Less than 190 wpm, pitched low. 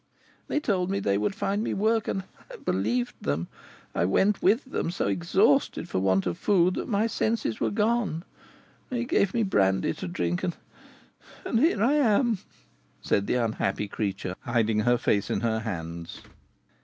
Yes: average, 170 wpm; low, 125 Hz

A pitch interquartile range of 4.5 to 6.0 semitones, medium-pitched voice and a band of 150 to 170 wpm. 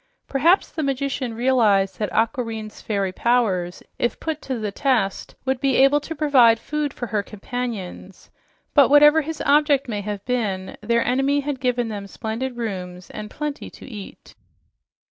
No: average, 4.8 semitones; high, 245 Hz; average, 160 wpm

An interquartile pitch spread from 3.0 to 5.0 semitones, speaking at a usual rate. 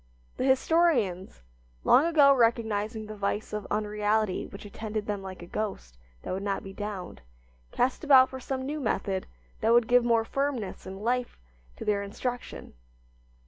Yes: average, 3.9 semitones; average, 160 wpm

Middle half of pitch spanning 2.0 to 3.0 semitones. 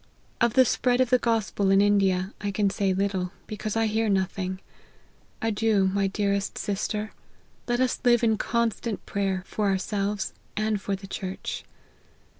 Yes: narrow, 2.4 semitones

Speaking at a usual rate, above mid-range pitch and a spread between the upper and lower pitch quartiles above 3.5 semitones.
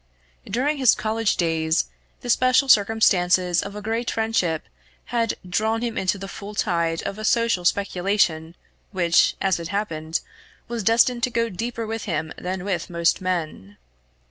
Yes: average, 155 wpm; high, 200 Hz; average, 4.6 semitones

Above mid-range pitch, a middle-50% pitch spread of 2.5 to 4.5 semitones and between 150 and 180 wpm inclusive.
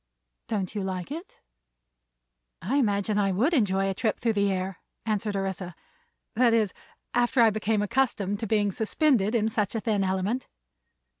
Yes: high, 210 Hz; average, 2.9 semitones; average, 160 wpm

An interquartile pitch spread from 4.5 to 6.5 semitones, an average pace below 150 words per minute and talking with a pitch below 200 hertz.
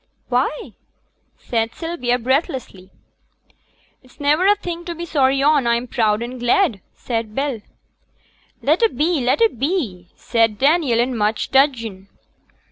No: average, 5.1 semitones; slow, 135 wpm; very high, 260 Hz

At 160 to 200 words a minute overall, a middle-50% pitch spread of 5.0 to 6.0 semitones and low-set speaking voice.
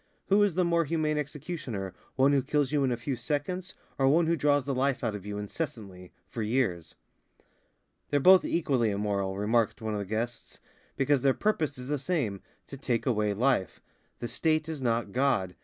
Yes: average, 190 wpm; wide, 5.6 semitones; low, 130 Hz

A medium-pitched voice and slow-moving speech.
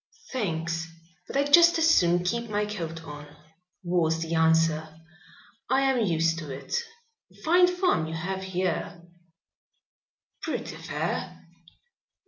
Yes: medium, 175 Hz; slow, 120 wpm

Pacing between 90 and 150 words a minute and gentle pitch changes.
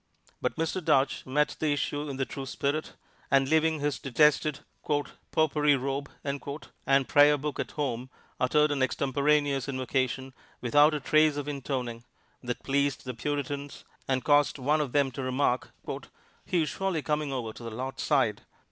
No: average, 160 wpm; narrow, 2.1 semitones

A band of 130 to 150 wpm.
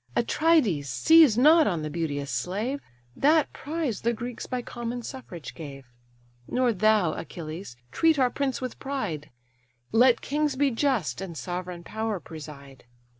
Yes: average, 140 wpm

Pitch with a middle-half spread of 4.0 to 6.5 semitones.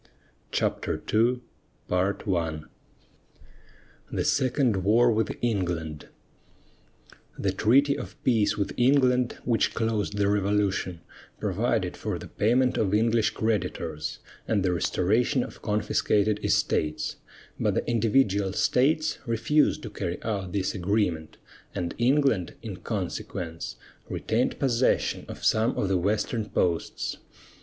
Yes: average, 4.3 semitones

